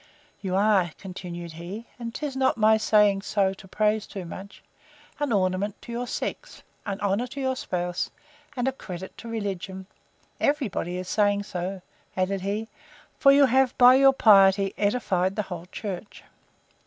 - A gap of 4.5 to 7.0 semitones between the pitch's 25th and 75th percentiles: No, average, 3.9 semitones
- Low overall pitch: No, high, 200 Hz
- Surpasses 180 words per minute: No, average, 155 wpm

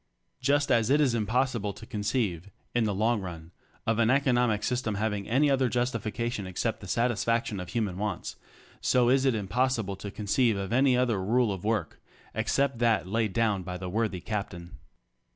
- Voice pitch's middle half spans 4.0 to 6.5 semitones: No, average, 3.6 semitones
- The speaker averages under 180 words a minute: No, average, 185 wpm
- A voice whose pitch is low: Yes, low, 110 Hz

